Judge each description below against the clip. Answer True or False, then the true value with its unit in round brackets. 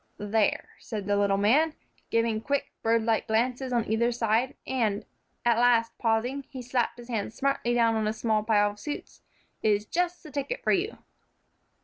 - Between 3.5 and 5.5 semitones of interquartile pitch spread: False (2.9 semitones)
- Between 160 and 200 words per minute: True (170 wpm)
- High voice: True (230 Hz)